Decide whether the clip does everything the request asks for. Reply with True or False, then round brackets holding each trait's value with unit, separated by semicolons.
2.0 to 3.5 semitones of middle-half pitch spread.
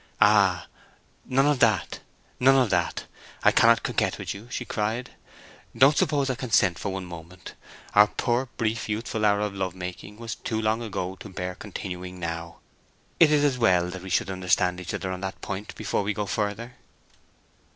False (4.1 semitones)